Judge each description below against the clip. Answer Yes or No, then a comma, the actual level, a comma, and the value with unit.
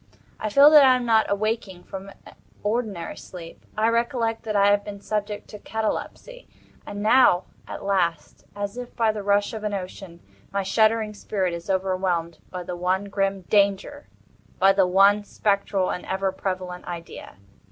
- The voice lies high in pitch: Yes, high, 200 Hz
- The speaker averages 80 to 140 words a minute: No, average, 165 wpm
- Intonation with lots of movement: No, narrow, 2.5 semitones